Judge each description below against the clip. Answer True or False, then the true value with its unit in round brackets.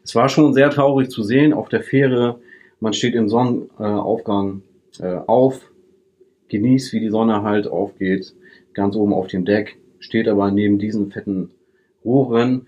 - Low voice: True (110 Hz)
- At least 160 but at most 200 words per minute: False (150 wpm)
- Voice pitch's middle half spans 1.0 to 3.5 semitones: False (4.5 semitones)